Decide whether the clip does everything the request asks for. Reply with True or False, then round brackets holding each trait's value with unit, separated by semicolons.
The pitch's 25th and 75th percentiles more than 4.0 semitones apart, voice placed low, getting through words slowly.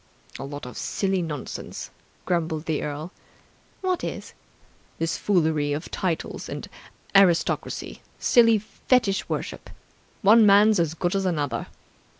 False (4.5 semitones; 175 Hz; 125 wpm)